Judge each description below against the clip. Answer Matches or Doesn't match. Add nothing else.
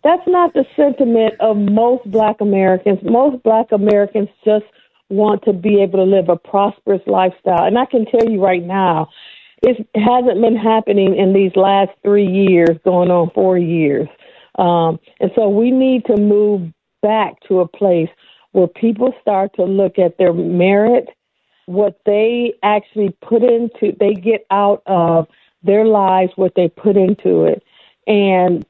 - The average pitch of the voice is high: Matches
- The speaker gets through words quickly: Doesn't match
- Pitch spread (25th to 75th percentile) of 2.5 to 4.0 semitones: Matches